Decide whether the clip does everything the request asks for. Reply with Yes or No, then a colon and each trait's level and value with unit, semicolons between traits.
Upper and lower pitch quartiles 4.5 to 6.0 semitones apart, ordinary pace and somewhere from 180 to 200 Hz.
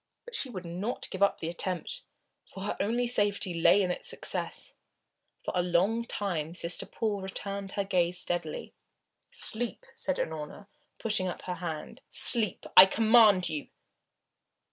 No: average, 3.7 semitones; average, 150 wpm; high, 190 Hz